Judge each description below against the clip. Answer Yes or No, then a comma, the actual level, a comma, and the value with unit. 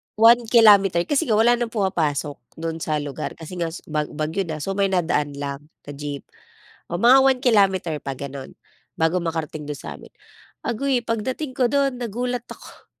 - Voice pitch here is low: No, medium, 185 Hz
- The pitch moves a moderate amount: No, wide, 7.6 semitones